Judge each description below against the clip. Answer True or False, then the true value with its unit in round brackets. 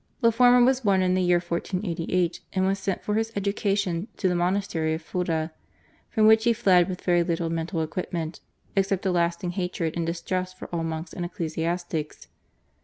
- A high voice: False (180 Hz)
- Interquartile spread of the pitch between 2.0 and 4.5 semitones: True (2.8 semitones)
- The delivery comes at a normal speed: True (180 wpm)